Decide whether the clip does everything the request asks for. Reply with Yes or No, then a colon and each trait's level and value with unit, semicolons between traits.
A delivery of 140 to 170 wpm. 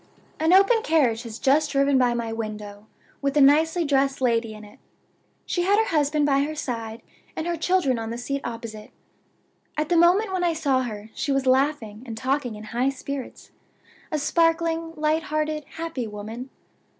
No: average, 180 wpm